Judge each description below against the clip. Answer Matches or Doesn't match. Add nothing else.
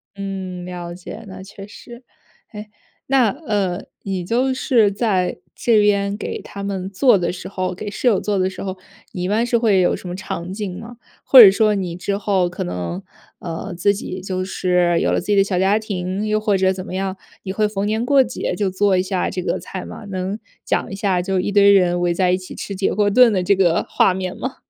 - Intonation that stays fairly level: Matches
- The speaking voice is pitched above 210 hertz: Doesn't match